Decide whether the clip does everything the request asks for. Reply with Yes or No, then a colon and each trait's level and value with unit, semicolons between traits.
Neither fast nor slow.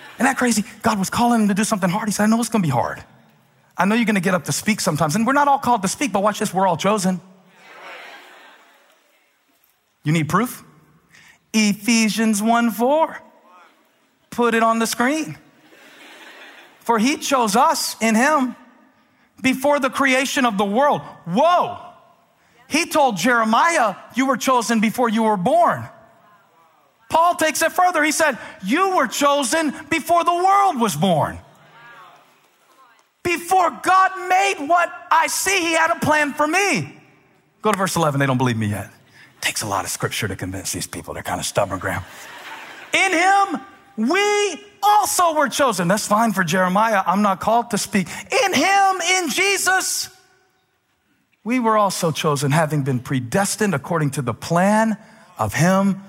Yes: average, 170 wpm